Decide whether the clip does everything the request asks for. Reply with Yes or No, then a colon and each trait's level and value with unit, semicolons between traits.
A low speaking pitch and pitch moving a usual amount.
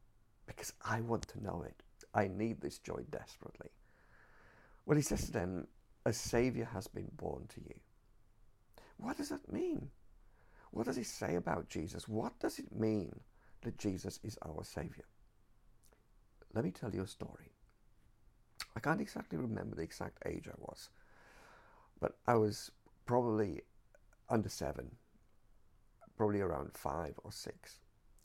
No: low, 110 Hz; narrow, 1.8 semitones